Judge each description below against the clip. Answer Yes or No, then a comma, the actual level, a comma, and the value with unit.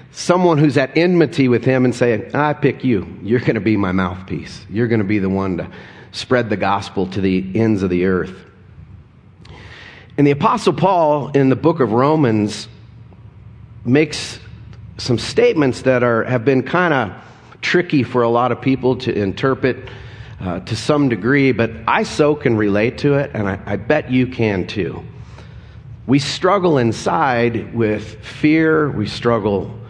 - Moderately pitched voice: No, low, 120 Hz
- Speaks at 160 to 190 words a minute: Yes, average, 170 wpm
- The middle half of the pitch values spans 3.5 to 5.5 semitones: Yes, average, 4.2 semitones